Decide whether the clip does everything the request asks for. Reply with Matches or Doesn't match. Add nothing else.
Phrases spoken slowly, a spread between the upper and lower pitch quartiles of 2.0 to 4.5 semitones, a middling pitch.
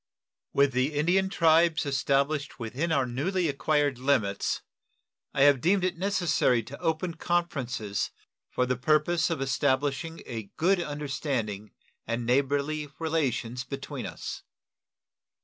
Matches